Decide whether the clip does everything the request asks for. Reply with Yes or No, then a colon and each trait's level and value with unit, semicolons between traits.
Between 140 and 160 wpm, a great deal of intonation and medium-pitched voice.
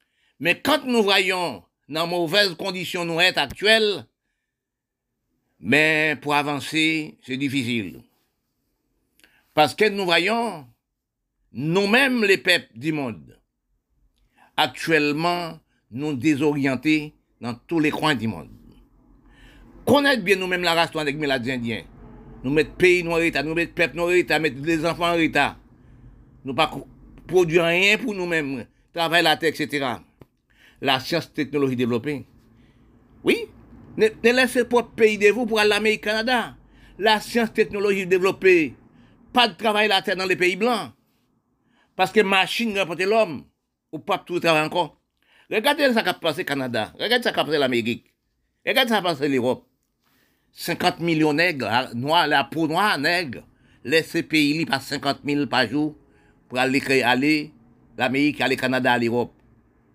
Yes: average, 150 wpm; wide, 6.3 semitones; medium, 155 Hz